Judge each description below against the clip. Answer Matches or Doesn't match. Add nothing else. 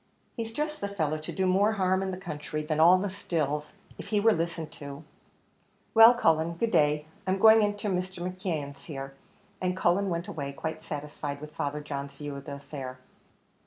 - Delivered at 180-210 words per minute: Matches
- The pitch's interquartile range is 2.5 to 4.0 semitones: Doesn't match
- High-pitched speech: Doesn't match